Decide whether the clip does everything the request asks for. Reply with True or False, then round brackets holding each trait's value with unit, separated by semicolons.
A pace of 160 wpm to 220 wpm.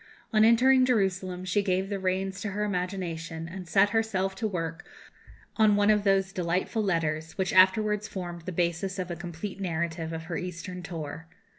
True (175 wpm)